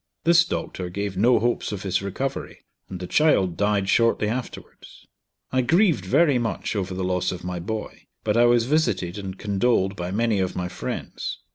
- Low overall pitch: Yes, low, 100 Hz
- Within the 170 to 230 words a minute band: Yes, average, 180 wpm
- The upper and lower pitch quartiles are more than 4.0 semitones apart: Yes, average, 4.5 semitones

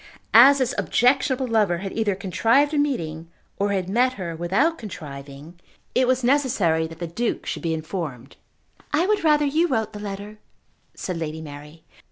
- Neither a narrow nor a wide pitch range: No, wide, 7.9 semitones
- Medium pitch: No, high, 200 Hz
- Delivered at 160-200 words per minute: Yes, average, 170 wpm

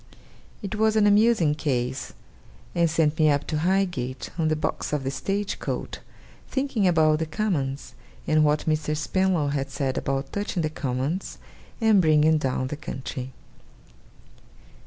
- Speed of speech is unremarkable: Yes, average, 150 wpm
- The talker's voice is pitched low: No, medium, 155 Hz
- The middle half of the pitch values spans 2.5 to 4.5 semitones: No, average, 5.1 semitones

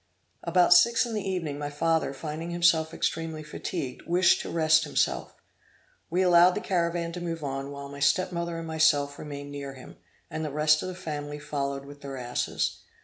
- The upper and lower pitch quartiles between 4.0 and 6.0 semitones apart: No, average, 3.2 semitones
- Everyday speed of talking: Yes, average, 190 wpm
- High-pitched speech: No, medium, 155 Hz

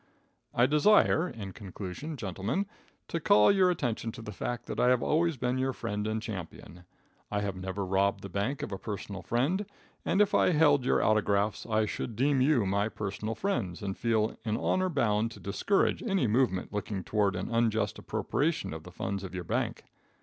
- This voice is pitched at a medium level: No, low, 110 Hz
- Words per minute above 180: Yes, average, 190 wpm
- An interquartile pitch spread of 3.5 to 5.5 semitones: Yes, average, 5.2 semitones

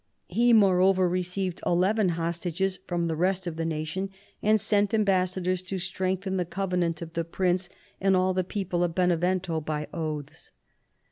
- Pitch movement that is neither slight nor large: No, narrow, 2.0 semitones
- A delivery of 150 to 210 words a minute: Yes, average, 160 wpm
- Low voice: No, medium, 180 Hz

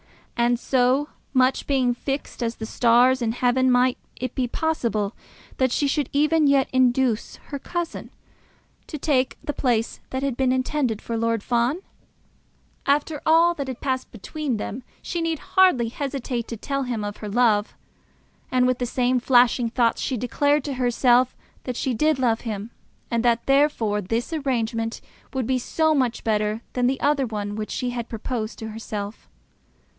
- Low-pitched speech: No, very high, 250 Hz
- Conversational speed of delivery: Yes, average, 170 wpm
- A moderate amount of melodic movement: Yes, average, 3.0 semitones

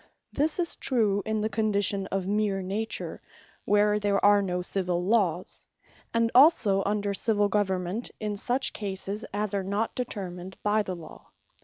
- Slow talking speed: No, average, 155 wpm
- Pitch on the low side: No, high, 205 Hz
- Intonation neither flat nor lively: No, narrow, 2.0 semitones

